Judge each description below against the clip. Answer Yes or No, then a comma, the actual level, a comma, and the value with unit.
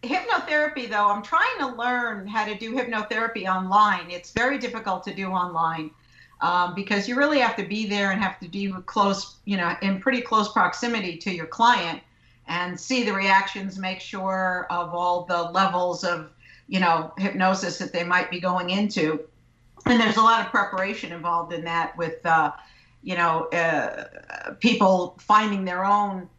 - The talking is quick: No, average, 175 wpm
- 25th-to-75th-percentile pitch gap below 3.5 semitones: No, average, 3.9 semitones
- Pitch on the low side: No, high, 195 Hz